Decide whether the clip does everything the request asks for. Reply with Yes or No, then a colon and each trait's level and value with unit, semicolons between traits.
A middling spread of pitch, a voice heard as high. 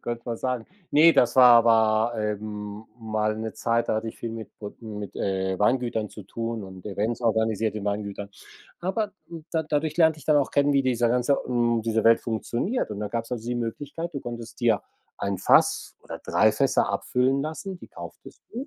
No: average, 3.5 semitones; low, 115 Hz